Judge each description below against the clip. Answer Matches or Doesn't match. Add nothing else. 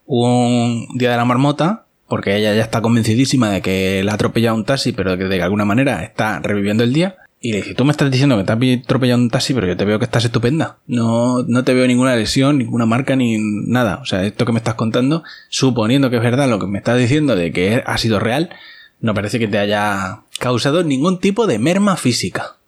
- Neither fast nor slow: Doesn't match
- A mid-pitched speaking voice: Doesn't match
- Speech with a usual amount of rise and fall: Matches